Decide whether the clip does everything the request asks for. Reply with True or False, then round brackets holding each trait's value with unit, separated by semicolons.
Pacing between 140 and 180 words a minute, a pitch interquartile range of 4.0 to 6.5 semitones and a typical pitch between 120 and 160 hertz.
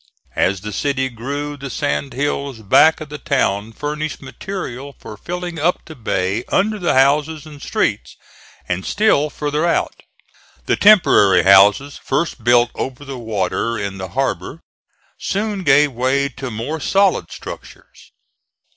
True (145 wpm; 5.2 semitones; 140 Hz)